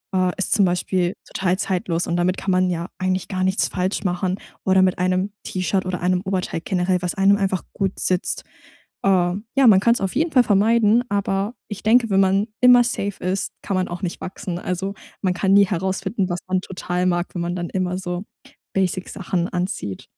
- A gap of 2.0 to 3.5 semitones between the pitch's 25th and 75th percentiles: No, narrow, 1.6 semitones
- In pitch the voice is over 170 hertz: Yes, medium, 185 Hz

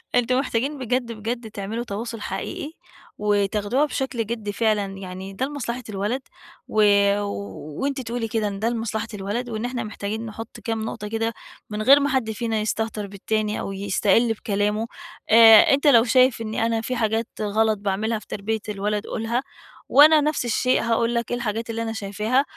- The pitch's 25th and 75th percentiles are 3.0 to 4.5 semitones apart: No, narrow, 2.4 semitones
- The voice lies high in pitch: Yes, high, 225 Hz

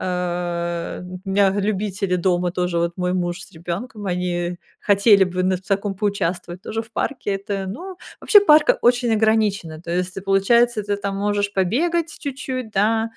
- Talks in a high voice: Yes, high, 195 Hz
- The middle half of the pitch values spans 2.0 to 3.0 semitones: No, average, 3.4 semitones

